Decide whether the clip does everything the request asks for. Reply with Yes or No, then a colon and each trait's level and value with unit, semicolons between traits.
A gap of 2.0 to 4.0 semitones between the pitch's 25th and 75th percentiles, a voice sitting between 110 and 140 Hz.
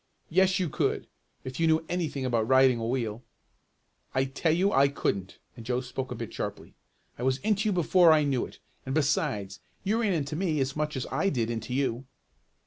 No: average, 4.6 semitones; low, 135 Hz